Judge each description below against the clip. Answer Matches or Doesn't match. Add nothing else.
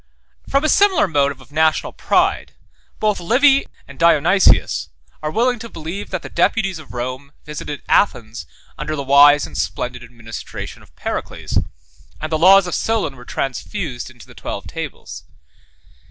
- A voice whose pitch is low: Doesn't match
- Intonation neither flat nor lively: Doesn't match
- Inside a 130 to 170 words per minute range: Matches